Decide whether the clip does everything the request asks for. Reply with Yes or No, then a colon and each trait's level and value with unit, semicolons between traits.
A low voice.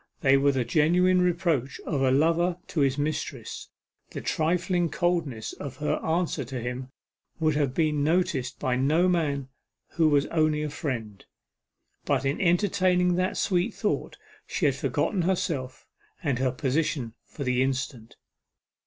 No: medium, 150 Hz